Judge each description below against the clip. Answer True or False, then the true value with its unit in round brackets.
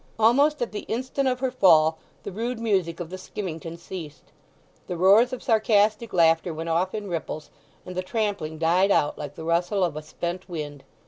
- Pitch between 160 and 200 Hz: True (185 Hz)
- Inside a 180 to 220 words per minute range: True (190 wpm)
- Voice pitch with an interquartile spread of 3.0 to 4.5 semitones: False (5.0 semitones)